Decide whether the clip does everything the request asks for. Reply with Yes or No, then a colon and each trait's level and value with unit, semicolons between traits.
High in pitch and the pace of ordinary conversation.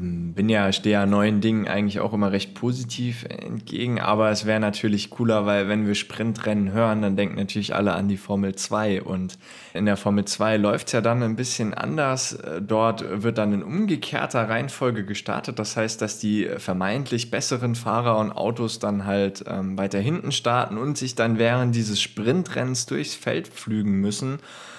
No: low, 110 Hz; average, 175 wpm